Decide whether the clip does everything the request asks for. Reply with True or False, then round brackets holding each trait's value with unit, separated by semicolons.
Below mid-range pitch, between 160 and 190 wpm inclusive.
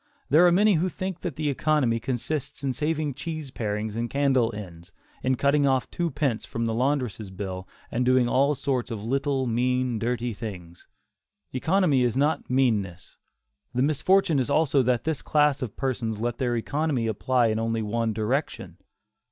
True (130 Hz; 170 wpm)